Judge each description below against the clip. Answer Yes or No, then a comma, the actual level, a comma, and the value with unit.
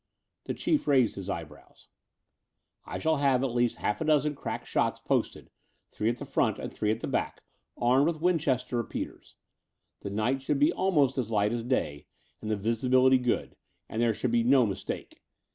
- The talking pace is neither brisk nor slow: Yes, average, 185 wpm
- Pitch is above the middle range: No, low, 125 Hz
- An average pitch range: Yes, average, 4.0 semitones